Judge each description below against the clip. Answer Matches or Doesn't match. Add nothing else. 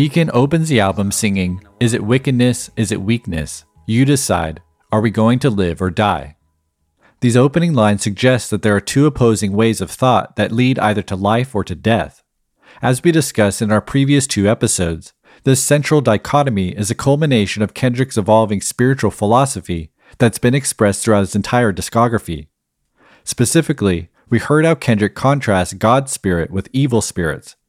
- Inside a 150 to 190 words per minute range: Matches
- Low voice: Matches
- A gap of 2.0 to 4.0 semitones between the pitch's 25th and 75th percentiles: Doesn't match